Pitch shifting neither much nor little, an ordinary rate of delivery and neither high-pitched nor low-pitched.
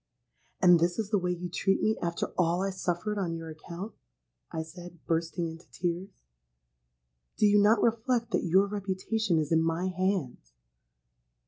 Yes: average, 3.3 semitones; average, 160 wpm; medium, 180 Hz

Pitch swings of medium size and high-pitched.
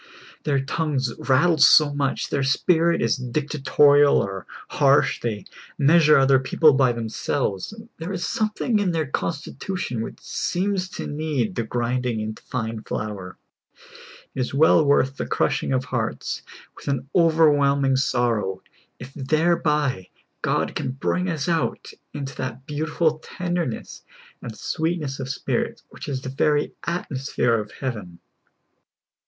No: average, 4.1 semitones; medium, 140 Hz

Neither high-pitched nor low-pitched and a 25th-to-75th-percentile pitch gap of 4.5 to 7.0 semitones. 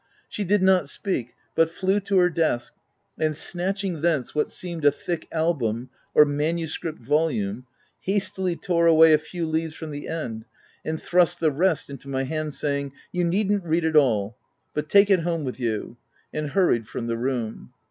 No: medium, 160 Hz; average, 4.1 semitones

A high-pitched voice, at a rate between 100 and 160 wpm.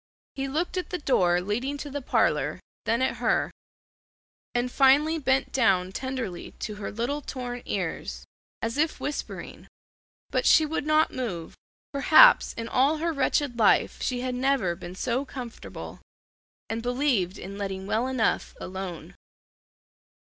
Yes: very high, 250 Hz; average, 145 wpm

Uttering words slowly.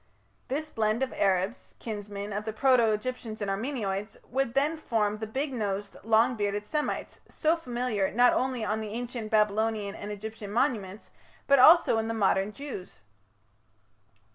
No: average, 155 wpm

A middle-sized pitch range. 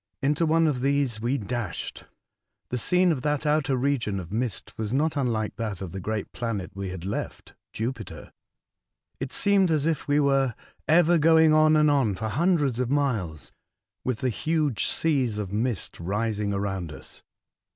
No: wide, 6.1 semitones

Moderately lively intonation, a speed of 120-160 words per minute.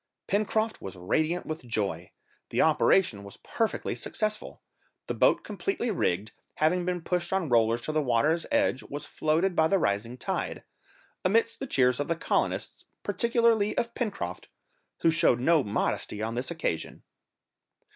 No: wide, 9.0 semitones; average, 150 wpm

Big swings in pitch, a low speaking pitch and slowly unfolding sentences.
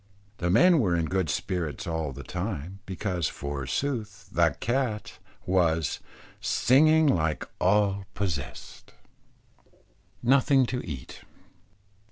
Yes: wide, 6.7 semitones; very low, 95 Hz; slow, 105 wpm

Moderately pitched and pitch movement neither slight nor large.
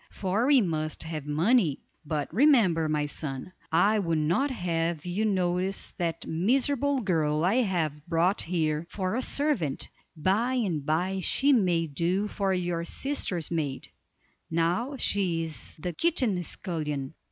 Yes: medium, 175 Hz; average, 4.9 semitones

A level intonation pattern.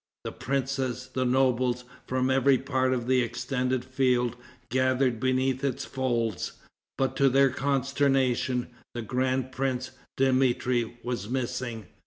Yes: narrow, 1.2 semitones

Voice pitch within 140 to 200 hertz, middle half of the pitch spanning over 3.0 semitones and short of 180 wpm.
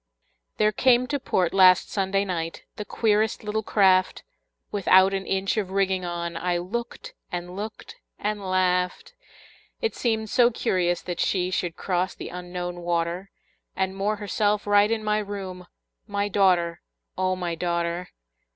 No: high, 190 Hz; average, 2.7 semitones; average, 150 wpm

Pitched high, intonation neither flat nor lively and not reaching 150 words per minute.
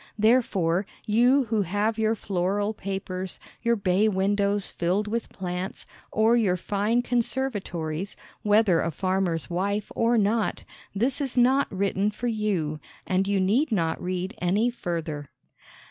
Yes: high, 200 Hz; average, 3.4 semitones; slow, 135 wpm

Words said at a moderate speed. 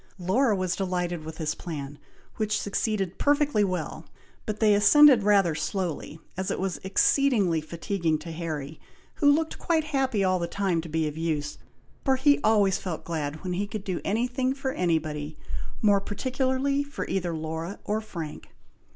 Yes: average, 170 wpm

